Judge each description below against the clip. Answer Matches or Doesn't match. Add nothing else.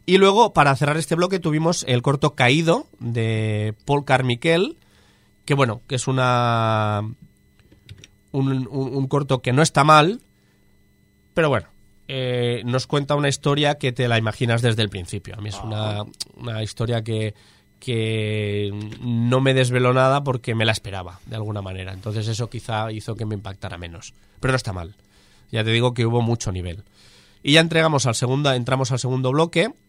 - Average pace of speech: Matches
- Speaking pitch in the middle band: Doesn't match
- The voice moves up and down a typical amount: Matches